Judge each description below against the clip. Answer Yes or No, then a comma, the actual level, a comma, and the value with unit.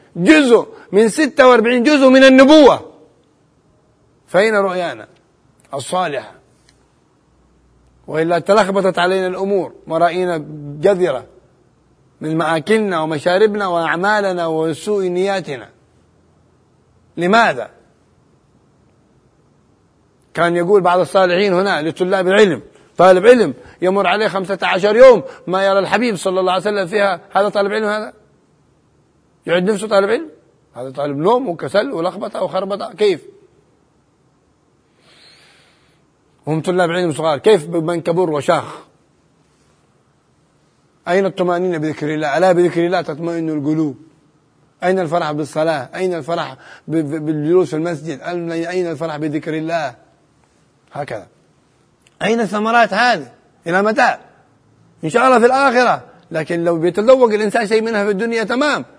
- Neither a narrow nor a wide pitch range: Yes, average, 4.6 semitones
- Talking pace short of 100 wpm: No, average, 110 wpm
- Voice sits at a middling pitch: Yes, medium, 180 Hz